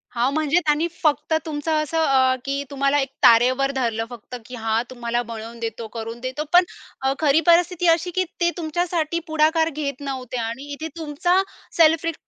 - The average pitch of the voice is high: Yes, very high, 280 Hz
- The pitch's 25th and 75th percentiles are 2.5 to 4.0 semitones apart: No, average, 4.6 semitones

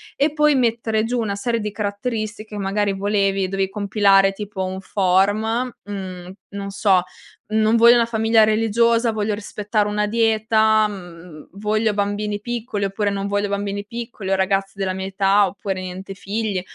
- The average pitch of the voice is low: No, high, 205 Hz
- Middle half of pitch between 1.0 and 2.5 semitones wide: Yes, narrow, 2.1 semitones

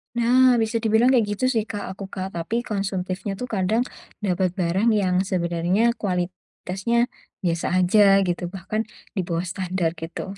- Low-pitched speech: No, high, 190 Hz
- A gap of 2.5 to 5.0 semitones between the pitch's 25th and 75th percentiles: Yes, average, 3.5 semitones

